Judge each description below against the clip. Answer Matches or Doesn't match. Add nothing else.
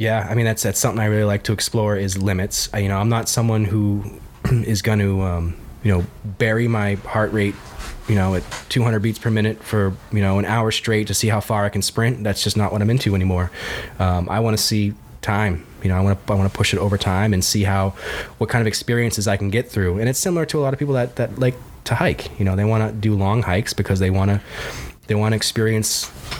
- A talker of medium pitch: Doesn't match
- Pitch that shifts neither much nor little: Doesn't match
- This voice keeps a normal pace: Doesn't match